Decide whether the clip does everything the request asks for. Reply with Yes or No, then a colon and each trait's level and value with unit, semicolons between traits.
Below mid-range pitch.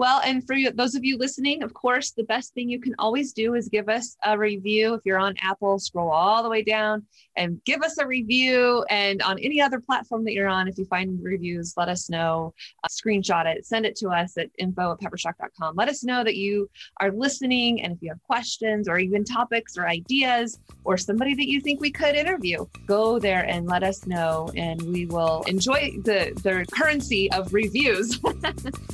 No: high, 215 Hz